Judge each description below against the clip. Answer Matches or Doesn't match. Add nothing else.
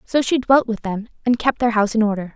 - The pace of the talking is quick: Matches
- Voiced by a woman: Matches